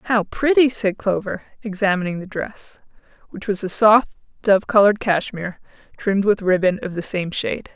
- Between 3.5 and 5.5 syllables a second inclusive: Yes, 5.3 syllables/s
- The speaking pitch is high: Yes, high, 200 Hz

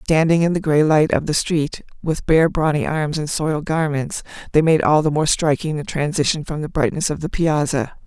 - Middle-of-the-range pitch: Yes, medium, 155 Hz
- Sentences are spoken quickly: Yes, fast, 215 wpm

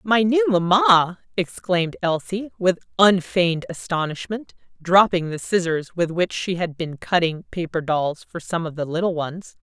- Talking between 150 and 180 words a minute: Yes, average, 155 wpm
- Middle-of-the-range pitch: Yes, medium, 180 Hz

